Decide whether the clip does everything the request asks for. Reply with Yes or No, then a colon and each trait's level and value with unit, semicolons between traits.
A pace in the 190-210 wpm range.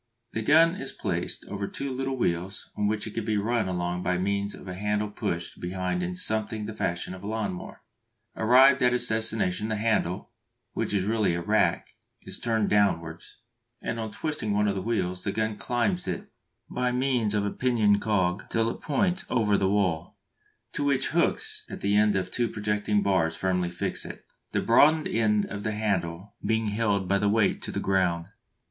Yes: average, 195 wpm